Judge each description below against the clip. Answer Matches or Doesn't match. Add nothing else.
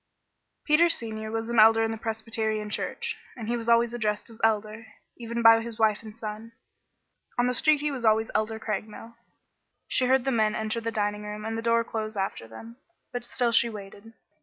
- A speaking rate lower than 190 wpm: Doesn't match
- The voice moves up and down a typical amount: Doesn't match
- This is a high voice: Matches